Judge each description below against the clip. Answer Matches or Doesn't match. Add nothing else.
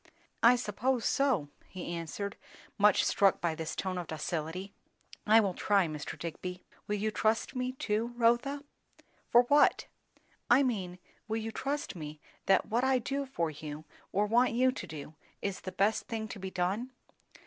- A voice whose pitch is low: Doesn't match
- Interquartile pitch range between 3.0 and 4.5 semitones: Doesn't match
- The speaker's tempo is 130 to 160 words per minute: Doesn't match